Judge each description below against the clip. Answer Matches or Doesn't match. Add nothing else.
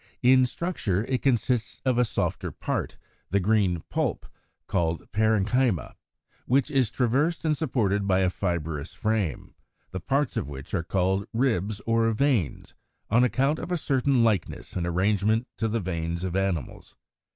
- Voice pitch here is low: Matches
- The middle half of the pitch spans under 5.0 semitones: Doesn't match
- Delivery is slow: Doesn't match